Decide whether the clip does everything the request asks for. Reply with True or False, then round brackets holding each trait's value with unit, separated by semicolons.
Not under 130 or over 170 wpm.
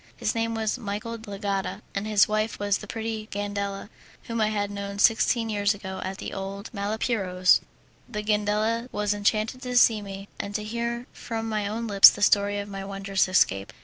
False (190 wpm)